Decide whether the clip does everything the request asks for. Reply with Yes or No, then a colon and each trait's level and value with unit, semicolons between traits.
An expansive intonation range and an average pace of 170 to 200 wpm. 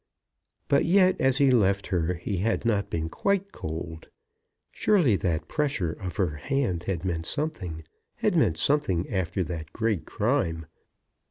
No: wide, 8.4 semitones; average, 150 wpm